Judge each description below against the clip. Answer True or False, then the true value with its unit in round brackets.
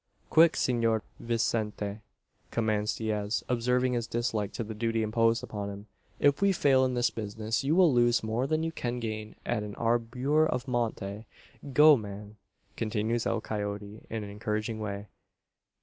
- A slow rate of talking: False (160 wpm)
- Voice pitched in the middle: False (115 Hz)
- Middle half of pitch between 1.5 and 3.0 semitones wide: True (2.7 semitones)